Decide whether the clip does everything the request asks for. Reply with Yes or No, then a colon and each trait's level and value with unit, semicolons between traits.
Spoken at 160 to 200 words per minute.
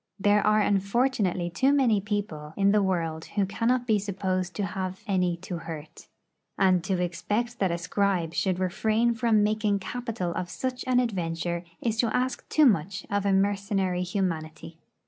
Yes: average, 165 wpm